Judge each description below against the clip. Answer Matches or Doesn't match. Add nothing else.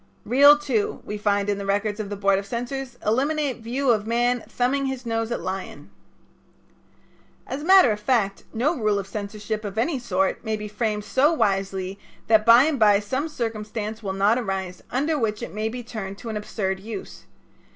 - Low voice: Doesn't match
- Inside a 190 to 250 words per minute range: Matches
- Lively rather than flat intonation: Doesn't match